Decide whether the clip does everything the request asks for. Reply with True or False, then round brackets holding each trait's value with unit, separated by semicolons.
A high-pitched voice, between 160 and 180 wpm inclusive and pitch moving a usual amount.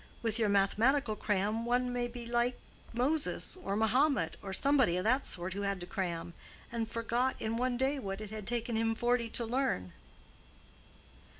True (230 Hz; 175 wpm; 3.5 semitones)